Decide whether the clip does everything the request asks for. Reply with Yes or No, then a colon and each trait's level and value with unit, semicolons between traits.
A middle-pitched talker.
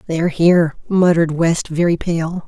Yes: medium, 165 Hz